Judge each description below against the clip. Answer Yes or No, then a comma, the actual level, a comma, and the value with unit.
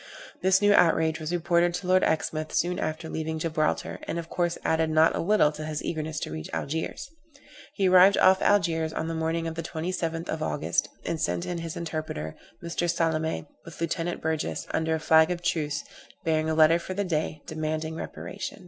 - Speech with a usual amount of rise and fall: No, narrow, 1.7 semitones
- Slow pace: No, average, 195 wpm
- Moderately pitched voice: Yes, medium, 160 Hz